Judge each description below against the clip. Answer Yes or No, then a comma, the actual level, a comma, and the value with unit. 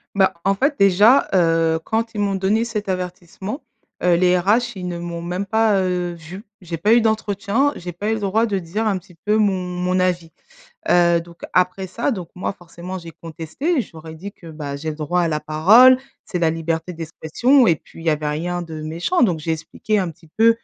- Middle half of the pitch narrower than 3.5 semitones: No, average, 4.0 semitones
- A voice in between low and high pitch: Yes, medium, 180 Hz